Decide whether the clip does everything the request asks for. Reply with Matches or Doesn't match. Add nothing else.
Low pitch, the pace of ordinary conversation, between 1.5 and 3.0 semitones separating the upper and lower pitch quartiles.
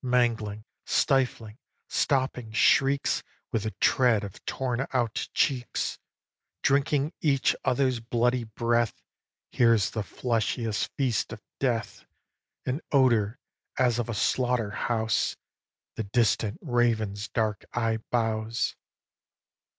Doesn't match